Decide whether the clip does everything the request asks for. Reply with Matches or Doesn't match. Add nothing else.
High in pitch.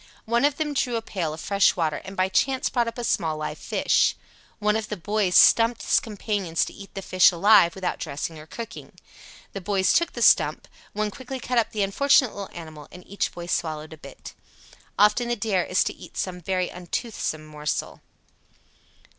Matches